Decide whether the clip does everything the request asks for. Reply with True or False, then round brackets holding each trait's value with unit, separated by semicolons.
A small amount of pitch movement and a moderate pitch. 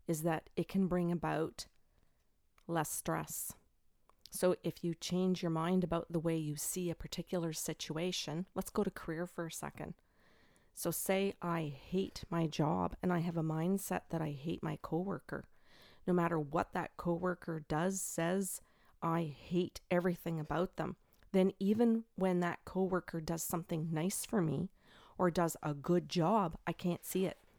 True (2.0 semitones; 175 Hz)